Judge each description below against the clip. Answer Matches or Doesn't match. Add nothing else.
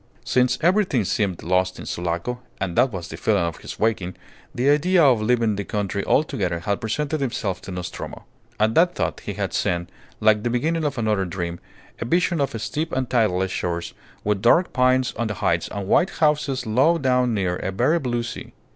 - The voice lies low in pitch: Matches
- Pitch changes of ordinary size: Doesn't match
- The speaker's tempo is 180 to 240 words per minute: Matches